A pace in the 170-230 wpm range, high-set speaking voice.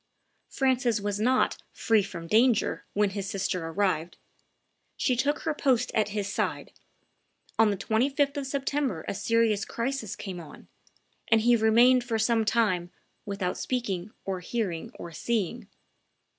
No: average, 145 wpm; high, 220 Hz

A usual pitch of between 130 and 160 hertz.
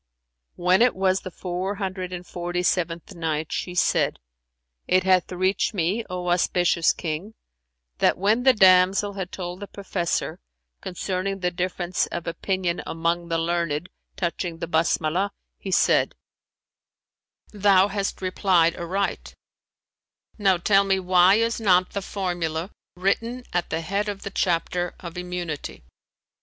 No: medium, 180 Hz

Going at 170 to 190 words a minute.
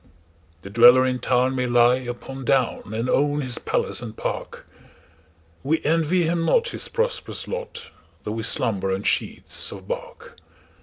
No: average, 140 wpm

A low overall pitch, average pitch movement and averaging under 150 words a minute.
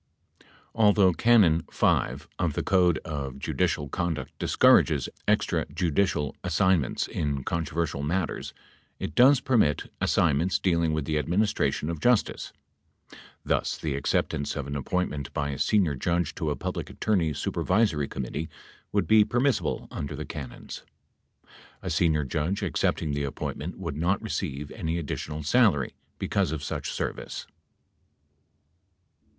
Yes: very low, 80 Hz; average, 4.4 semitones; slow, 135 wpm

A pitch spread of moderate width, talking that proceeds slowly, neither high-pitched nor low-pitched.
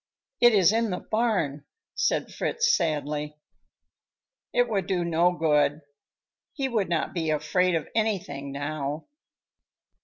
No: wide, 6.2 semitones; slow, 125 wpm; medium, 170 Hz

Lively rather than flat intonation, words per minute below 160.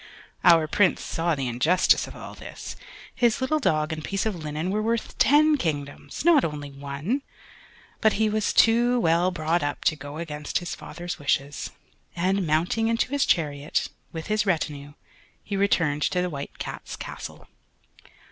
No: wide, 6.3 semitones; average, 165 wpm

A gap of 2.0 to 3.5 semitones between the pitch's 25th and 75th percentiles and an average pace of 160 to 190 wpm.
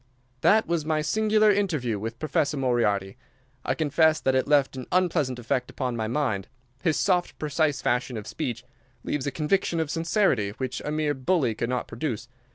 No: average, 4.8 semitones; average, 175 wpm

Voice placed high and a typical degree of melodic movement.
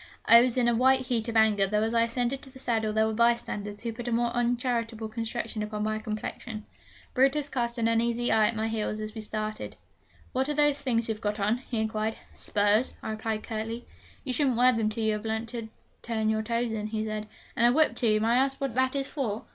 No: high, 230 Hz; narrow, 2.1 semitones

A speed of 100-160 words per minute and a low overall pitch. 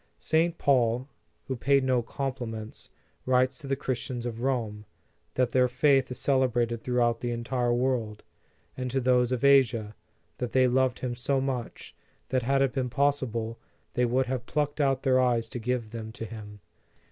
No: average, 175 wpm; low, 125 Hz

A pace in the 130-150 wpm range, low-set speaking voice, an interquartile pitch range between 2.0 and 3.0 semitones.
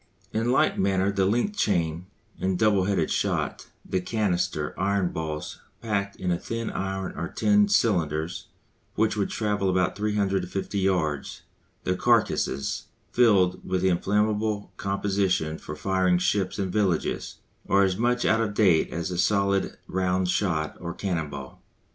Yes: average, 140 wpm; very low, 95 Hz; narrow, 2.4 semitones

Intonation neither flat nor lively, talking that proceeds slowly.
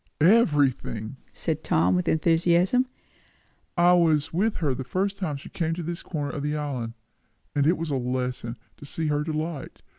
No: average, 4.2 semitones; average, 175 wpm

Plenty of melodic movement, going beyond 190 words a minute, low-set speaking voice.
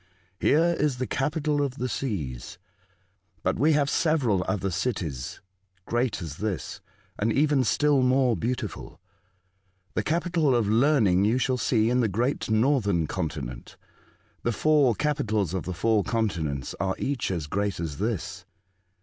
No: wide, 6.5 semitones; average, 150 wpm; low, 115 Hz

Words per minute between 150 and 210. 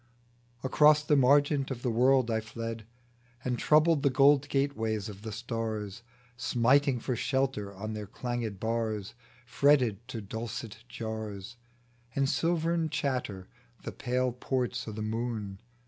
No: slow, 135 wpm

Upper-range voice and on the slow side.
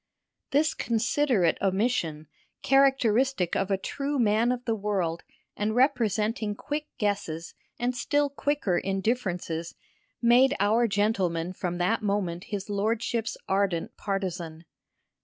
Yes: high, 210 Hz; slow, 115 wpm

